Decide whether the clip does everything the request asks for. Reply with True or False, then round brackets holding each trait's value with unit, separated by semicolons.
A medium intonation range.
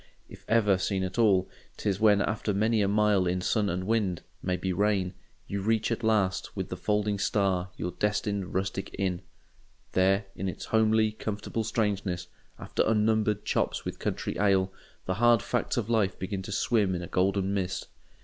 False (2.3 semitones)